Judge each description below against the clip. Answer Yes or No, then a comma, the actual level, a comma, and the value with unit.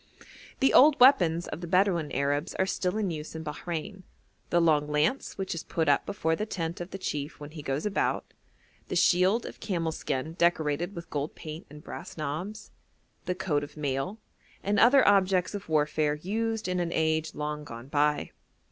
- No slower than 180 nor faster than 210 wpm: Yes, average, 185 wpm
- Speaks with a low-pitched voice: No, medium, 165 Hz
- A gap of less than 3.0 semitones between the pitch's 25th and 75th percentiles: No, average, 4.3 semitones